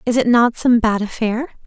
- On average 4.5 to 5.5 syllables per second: Yes, 5.0 syllables/s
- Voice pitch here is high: Yes, high, 235 Hz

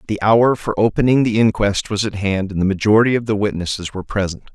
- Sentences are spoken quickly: Yes, fast, 225 wpm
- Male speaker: Yes, male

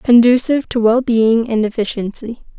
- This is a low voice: No, high, 230 Hz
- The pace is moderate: No, slow, 115 wpm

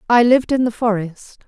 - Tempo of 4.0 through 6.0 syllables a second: Yes, 5.5 syllables/s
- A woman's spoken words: Yes, female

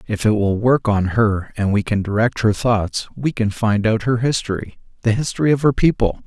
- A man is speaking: Yes, male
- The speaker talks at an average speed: No, fast, 220 wpm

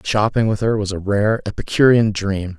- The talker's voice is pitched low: Yes, low, 105 Hz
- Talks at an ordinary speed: Yes, average, 185 wpm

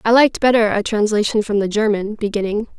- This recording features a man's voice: No, female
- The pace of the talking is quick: No, average, 195 wpm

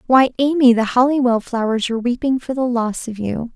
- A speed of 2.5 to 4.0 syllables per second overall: No, 5.5 syllables/s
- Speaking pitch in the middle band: No, high, 245 Hz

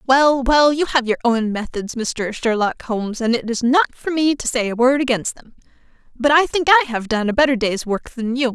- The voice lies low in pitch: No, very high, 250 Hz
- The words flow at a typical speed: No, fast, 240 wpm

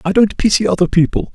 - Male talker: Yes, male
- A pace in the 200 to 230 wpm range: Yes, fast, 225 wpm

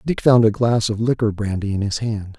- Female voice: No, male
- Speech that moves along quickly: Yes, fast, 250 wpm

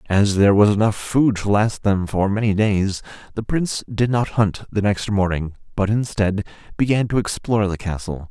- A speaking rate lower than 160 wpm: No, average, 190 wpm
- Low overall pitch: Yes, low, 105 Hz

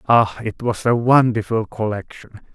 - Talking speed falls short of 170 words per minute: Yes, average, 140 wpm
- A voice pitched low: Yes, low, 115 Hz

